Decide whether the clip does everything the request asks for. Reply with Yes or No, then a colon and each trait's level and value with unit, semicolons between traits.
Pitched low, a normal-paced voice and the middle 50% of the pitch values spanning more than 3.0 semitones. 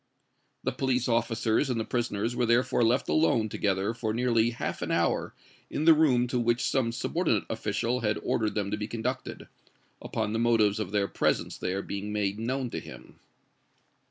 No: low, 115 Hz; average, 180 wpm; average, 2.7 semitones